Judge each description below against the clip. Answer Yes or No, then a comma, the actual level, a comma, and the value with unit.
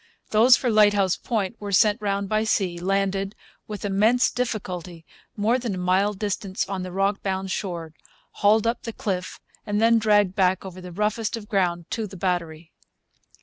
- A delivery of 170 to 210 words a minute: Yes, average, 175 wpm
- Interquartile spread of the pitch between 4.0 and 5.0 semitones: No, narrow, 2.5 semitones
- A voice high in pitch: Yes, high, 200 Hz